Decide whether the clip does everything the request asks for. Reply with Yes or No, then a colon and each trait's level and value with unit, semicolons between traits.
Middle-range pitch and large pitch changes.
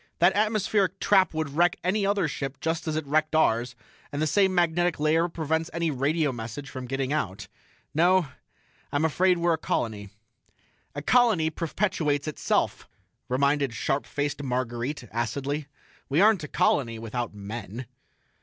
No: medium, 150 Hz; average, 4.8 semitones